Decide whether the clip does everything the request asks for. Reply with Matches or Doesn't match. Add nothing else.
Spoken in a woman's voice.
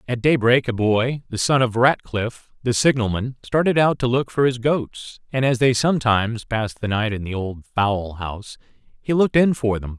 Doesn't match